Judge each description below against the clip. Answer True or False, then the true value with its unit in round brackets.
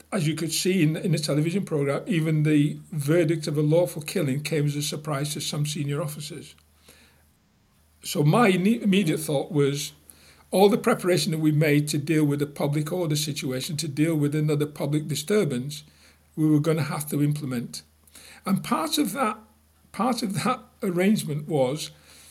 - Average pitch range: True (3.4 semitones)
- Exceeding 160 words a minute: True (170 wpm)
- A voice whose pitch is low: False (155 Hz)